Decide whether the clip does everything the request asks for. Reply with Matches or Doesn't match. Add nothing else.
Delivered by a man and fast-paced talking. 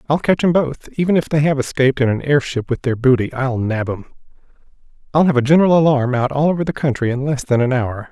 Matches